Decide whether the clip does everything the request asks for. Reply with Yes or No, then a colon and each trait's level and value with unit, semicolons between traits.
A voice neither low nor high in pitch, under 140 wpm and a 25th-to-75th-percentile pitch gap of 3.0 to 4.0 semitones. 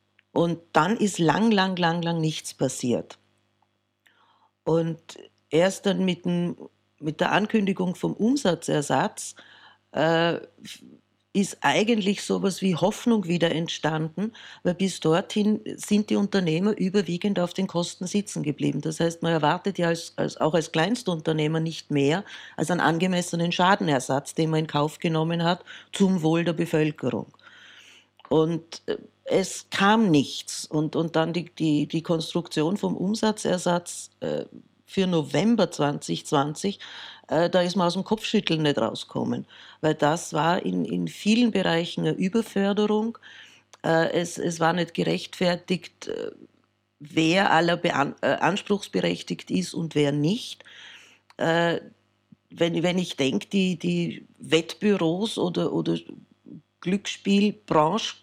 Yes: medium, 170 Hz; average, 130 wpm; average, 3.7 semitones